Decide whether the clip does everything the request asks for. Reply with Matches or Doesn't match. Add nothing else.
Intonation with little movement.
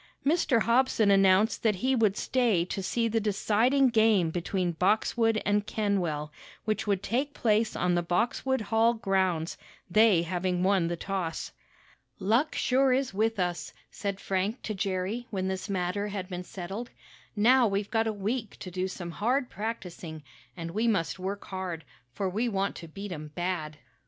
Doesn't match